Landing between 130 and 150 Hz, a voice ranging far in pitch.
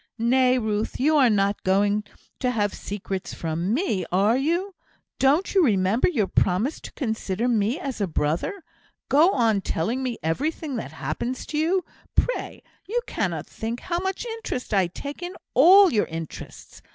No: high, 240 Hz; wide, 7.6 semitones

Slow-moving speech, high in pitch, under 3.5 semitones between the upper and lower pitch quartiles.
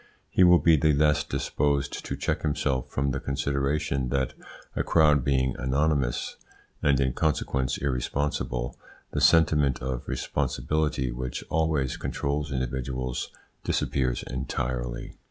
No: slow, 120 wpm; very low, 70 Hz; narrow, 2.5 semitones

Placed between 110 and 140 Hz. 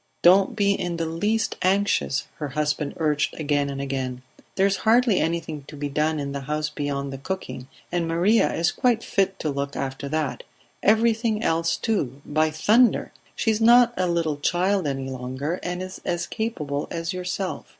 No: medium, 165 Hz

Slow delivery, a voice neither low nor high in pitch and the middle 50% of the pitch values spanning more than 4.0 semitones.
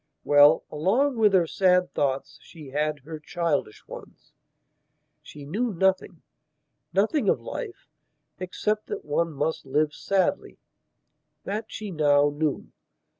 Yes: slow, 120 wpm; medium, 160 Hz; average, 4.9 semitones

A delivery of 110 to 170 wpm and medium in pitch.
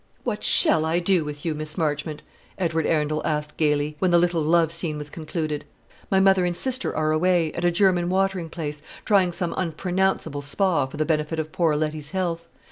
No: average, 195 wpm; medium, 165 Hz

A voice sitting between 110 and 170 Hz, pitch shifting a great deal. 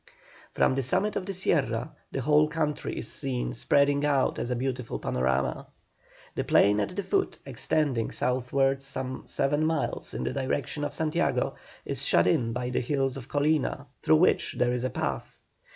No: low, 135 Hz; average, 3.2 semitones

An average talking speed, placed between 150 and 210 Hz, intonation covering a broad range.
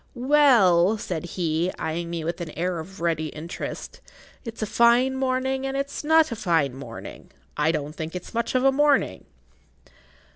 Yes: average, 170 wpm; medium, 185 Hz; wide, 8.0 semitones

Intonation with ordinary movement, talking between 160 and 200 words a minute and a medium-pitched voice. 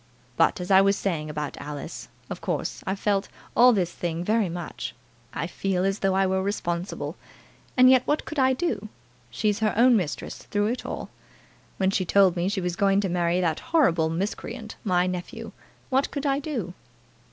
No: average, 3.8 semitones; average, 185 wpm; high, 195 Hz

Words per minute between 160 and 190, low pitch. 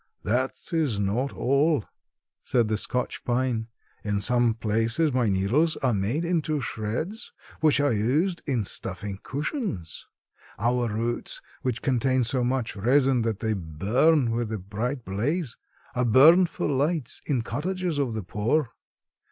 No: average, 145 wpm; low, 125 Hz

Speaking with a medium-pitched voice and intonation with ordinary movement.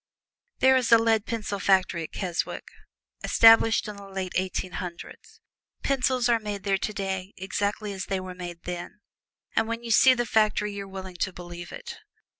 No: high, 200 Hz; average, 3.3 semitones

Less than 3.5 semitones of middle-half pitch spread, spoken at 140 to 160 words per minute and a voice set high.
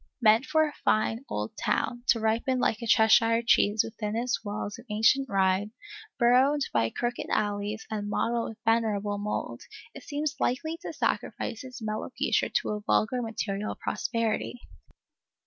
Yes: narrow, 2.5 semitones; average, 155 wpm; high, 225 Hz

